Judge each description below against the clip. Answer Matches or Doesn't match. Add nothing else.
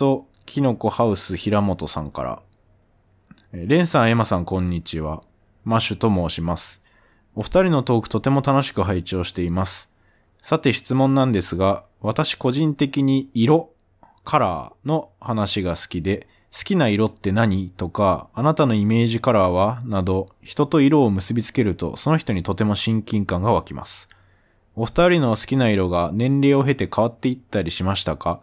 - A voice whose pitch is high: Doesn't match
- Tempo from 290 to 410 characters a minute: Matches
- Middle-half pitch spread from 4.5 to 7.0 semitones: Matches